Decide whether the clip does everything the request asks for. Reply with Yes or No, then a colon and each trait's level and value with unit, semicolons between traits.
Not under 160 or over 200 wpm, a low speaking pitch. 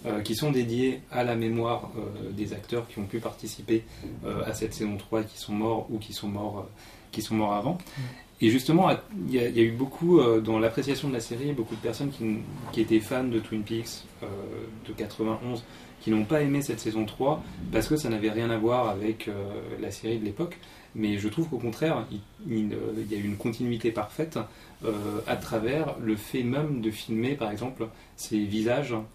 No: average, 210 wpm; low, 110 Hz